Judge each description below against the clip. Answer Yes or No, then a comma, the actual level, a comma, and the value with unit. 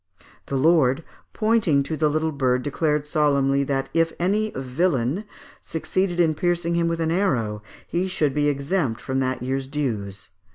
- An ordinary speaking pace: Yes, average, 160 wpm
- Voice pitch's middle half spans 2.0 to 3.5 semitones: No, average, 4.2 semitones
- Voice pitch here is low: No, medium, 150 Hz